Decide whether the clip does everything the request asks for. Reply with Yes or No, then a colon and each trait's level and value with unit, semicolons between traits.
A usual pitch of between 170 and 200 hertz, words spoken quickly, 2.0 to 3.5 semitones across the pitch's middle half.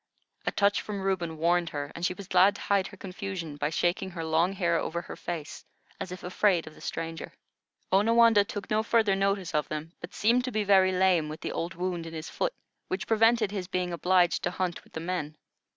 Yes: medium, 185 Hz; fast, 220 wpm; average, 3.1 semitones